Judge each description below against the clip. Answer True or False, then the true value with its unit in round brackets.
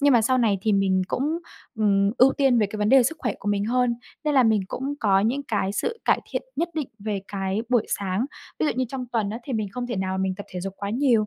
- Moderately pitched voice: False (220 Hz)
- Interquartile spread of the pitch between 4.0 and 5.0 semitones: True (4.4 semitones)